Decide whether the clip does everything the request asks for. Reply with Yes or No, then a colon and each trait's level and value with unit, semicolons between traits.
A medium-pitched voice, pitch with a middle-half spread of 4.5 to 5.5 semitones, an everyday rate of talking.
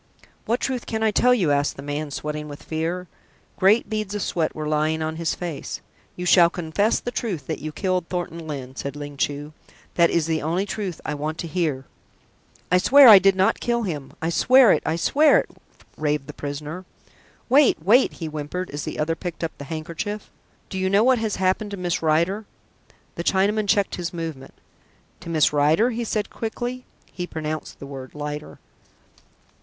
Yes: medium, 170 Hz; average, 5.1 semitones; average, 190 wpm